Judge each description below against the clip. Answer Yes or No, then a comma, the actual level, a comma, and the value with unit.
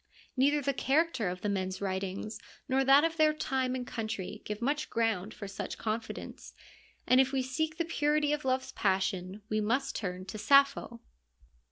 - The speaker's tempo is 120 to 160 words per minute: No, average, 180 wpm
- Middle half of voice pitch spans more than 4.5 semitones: Yes, wide, 5.6 semitones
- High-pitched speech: Yes, very high, 250 Hz